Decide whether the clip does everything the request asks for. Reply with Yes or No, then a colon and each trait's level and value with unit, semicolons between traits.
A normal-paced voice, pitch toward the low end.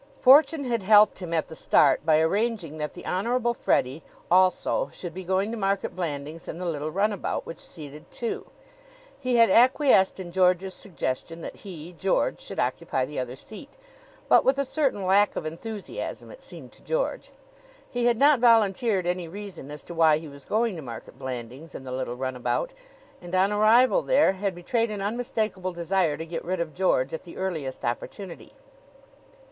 No: average, 180 wpm; medium, 185 Hz